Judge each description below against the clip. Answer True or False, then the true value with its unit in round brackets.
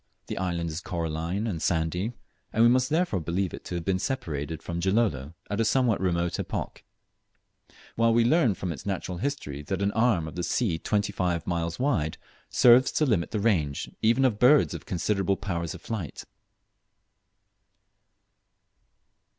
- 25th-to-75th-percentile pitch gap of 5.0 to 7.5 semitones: True (5.4 semitones)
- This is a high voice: False (95 Hz)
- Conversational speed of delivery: True (165 wpm)